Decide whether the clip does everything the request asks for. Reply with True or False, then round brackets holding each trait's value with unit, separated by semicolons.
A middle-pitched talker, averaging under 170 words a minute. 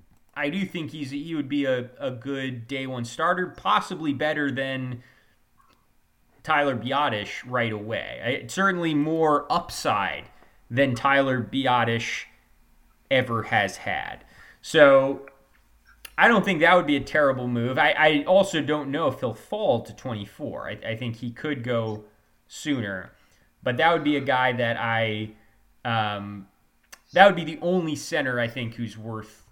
False (130 Hz; 155 wpm)